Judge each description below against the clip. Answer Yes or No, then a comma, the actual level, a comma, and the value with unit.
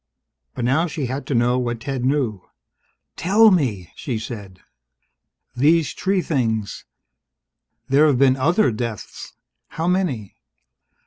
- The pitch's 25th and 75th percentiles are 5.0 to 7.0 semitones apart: Yes, average, 5.3 semitones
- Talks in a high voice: No, low, 130 Hz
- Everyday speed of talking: No, slow, 125 wpm